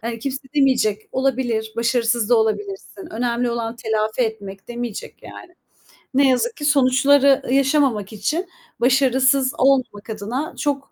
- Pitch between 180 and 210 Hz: No, high, 245 Hz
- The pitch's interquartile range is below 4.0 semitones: Yes, average, 3.6 semitones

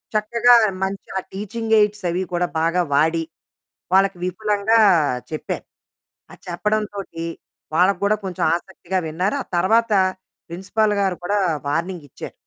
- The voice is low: No, high, 190 Hz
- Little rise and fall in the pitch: No, average, 3.3 semitones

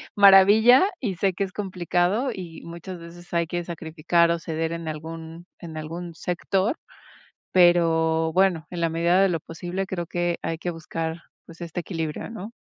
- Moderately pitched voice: Yes, medium, 170 Hz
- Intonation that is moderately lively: No, narrow, 2.2 semitones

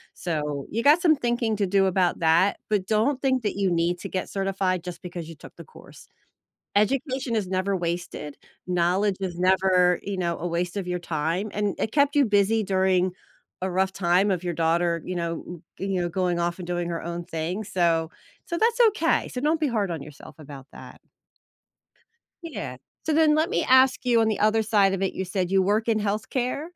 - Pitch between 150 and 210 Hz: Yes, high, 190 Hz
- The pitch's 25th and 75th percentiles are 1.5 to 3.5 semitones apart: No, average, 4.0 semitones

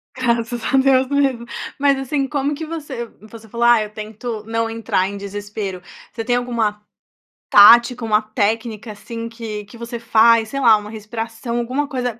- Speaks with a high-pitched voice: Yes, high, 230 Hz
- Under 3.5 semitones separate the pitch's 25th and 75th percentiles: Yes, narrow, 2.5 semitones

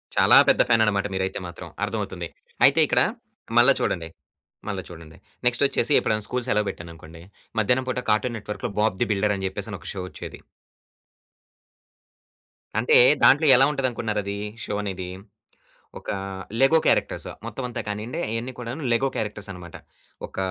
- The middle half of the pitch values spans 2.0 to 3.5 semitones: No, average, 4.3 semitones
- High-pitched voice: No, low, 105 Hz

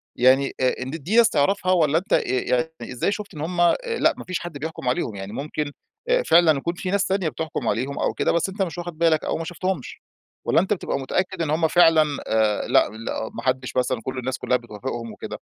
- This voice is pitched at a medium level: Yes, medium, 155 Hz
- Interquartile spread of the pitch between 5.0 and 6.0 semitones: Yes, wide, 5.4 semitones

